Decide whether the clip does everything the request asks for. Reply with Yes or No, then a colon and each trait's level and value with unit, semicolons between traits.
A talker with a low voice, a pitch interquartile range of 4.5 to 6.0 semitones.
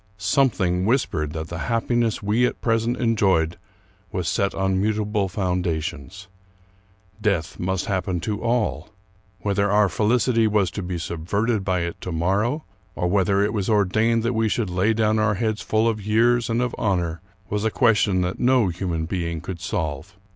No: low, 100 Hz; average, 3.9 semitones